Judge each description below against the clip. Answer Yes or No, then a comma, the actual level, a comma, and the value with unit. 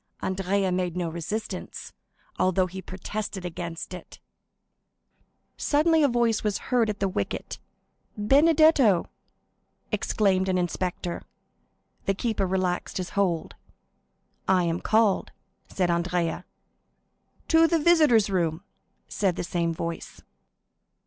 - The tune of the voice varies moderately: Yes, average, 3.7 semitones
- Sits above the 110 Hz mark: Yes, high, 190 Hz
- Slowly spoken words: Yes, slow, 110 wpm